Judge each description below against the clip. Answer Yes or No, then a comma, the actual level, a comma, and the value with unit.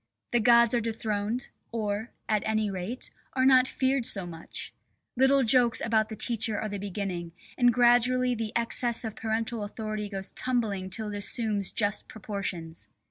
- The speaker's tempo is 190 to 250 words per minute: No, average, 160 wpm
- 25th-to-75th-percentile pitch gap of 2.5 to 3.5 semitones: Yes, average, 2.8 semitones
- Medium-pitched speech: No, high, 220 Hz